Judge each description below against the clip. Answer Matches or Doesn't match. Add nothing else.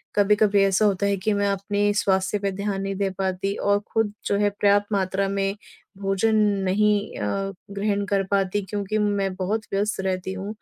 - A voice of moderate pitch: Doesn't match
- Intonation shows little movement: Matches